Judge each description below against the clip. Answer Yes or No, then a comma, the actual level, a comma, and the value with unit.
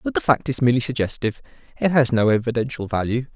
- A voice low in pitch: Yes, low, 120 Hz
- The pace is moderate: Yes, average, 195 wpm